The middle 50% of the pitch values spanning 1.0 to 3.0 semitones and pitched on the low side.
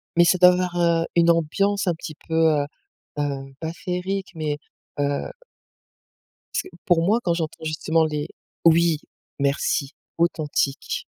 No: narrow, 2.5 semitones; medium, 165 Hz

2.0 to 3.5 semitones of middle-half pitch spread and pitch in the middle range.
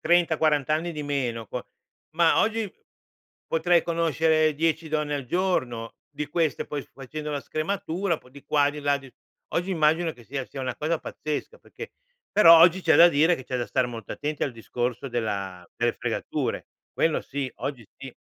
No: average, 3.9 semitones; medium, 150 Hz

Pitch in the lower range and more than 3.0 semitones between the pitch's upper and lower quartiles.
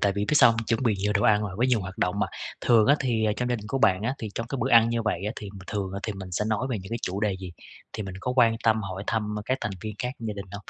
No: low, 105 Hz; narrow, 2.6 semitones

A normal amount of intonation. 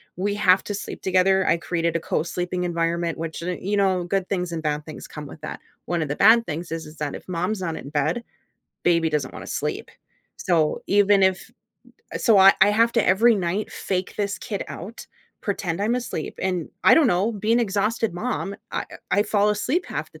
Yes: average, 3.5 semitones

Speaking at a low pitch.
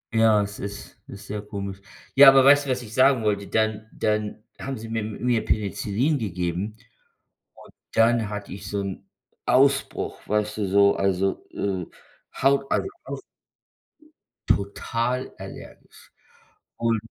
Yes: low, 105 Hz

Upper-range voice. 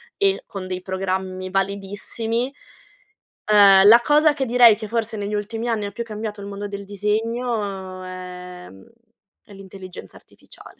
Yes: high, 205 Hz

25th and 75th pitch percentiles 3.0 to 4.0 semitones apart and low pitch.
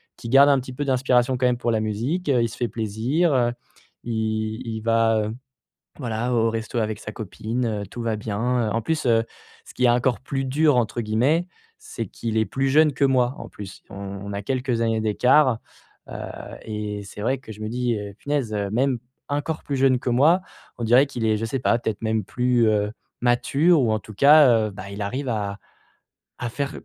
Yes: average, 3.3 semitones; low, 120 Hz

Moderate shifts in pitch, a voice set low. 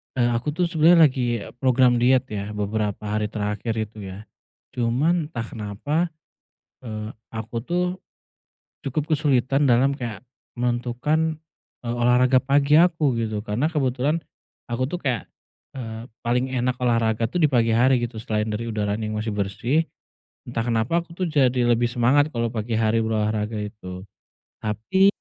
Yes: average, 3.9 semitones; low, 120 Hz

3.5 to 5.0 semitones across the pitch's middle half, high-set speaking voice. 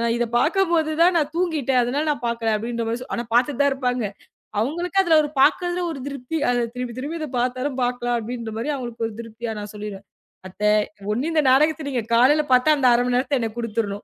Yes: average, 4.2 semitones; very high, 250 Hz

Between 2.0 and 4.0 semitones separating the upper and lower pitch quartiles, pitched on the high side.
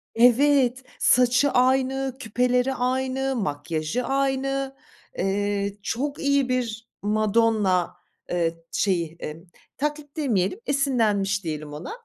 No: average, 5.3 semitones; high, 245 Hz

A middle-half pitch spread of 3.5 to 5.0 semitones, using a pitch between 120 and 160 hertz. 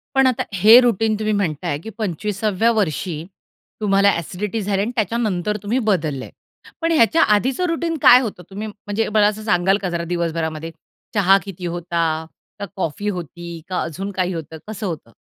No: average, 3.9 semitones; high, 195 Hz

